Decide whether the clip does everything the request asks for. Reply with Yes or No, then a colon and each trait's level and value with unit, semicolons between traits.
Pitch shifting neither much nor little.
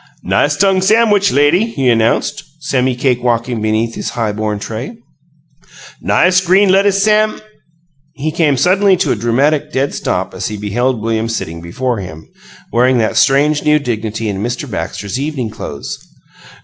No: wide, 7.0 semitones